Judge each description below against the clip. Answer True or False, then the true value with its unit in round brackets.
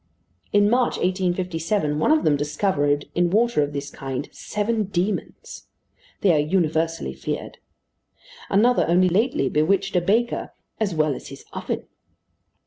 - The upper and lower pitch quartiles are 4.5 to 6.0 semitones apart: True (5.4 semitones)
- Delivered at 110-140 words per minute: True (135 wpm)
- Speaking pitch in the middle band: True (175 Hz)